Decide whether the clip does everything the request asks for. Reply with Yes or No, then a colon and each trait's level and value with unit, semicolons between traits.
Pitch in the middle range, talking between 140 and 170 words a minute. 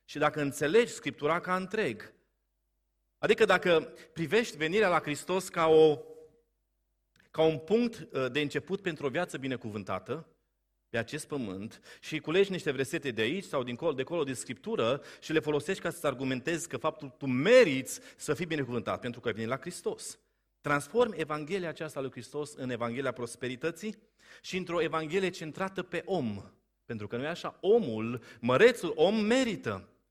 Yes: medium, 155 Hz; average, 160 wpm